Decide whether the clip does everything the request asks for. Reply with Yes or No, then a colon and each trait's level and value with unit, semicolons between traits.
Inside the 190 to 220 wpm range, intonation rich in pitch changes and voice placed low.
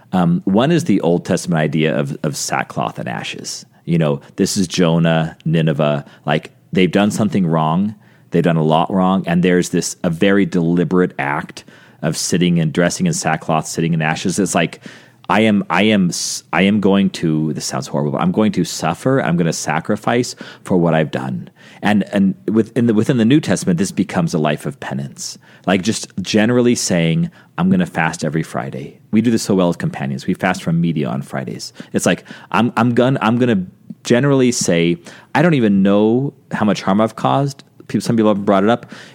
Yes: average, 200 wpm; wide, 6.0 semitones; very low, 95 Hz